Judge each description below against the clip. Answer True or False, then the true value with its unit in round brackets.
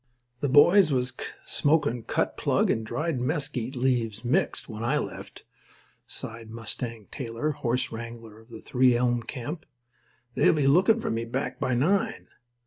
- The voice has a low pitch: True (125 Hz)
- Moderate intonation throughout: True (3.9 semitones)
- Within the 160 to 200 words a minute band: False (150 wpm)